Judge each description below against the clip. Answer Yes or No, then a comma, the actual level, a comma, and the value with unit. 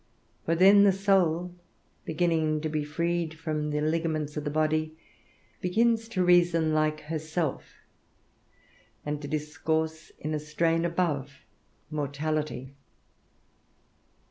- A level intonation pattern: Yes, narrow, 2.1 semitones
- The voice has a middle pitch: Yes, medium, 155 Hz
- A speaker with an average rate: No, slow, 115 wpm